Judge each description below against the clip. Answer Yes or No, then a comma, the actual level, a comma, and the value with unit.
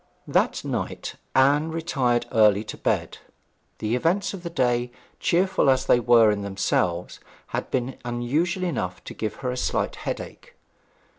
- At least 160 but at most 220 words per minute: No, average, 150 wpm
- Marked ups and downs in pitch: Yes, wide, 6.3 semitones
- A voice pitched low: Yes, low, 125 Hz